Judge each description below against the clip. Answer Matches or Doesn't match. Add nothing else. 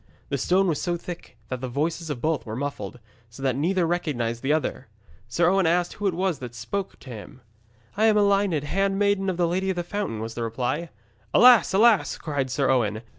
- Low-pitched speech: Doesn't match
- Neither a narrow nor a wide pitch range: Doesn't match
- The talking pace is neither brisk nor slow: Doesn't match